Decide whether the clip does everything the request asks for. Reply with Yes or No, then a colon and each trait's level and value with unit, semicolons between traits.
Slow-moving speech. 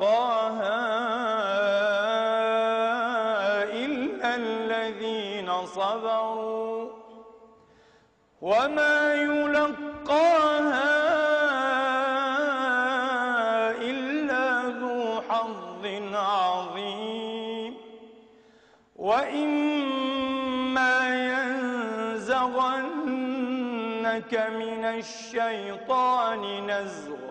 Yes: slow, 35 wpm